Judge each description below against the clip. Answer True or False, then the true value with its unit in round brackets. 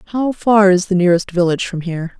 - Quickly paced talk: True (220 wpm)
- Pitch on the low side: False (190 Hz)